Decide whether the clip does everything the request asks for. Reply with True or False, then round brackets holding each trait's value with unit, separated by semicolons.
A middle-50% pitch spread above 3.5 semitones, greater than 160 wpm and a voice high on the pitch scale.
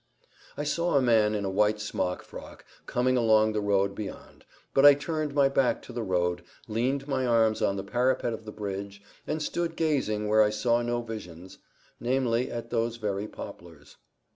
False (3.9 semitones; 185 wpm; 115 Hz)